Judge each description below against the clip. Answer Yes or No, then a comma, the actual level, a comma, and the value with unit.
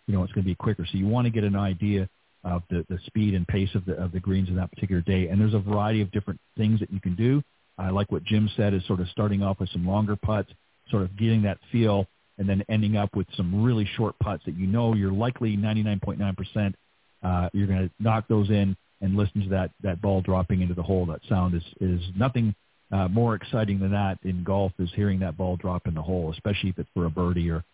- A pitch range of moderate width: No, narrow, 2.3 semitones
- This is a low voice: Yes, low, 100 Hz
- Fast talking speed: Yes, fast, 260 wpm